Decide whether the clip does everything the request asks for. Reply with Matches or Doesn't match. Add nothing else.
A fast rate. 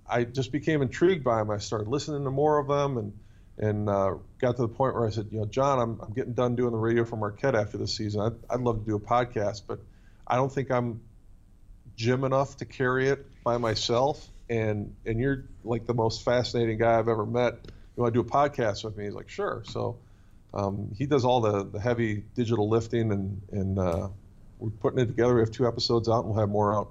Matches